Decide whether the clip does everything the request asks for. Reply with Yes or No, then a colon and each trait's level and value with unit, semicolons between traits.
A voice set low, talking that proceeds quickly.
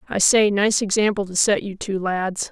No: high, 200 Hz; fast, 215 wpm